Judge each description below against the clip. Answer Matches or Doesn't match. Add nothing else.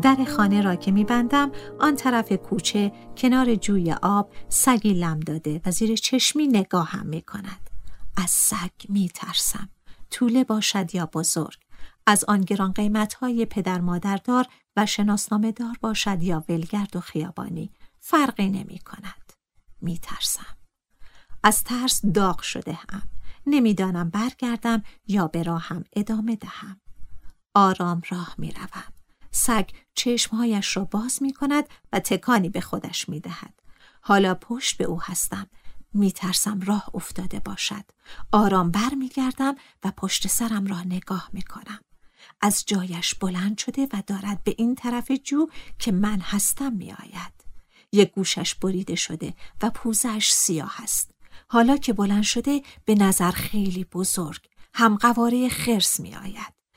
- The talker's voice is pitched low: Doesn't match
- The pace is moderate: Matches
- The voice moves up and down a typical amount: Matches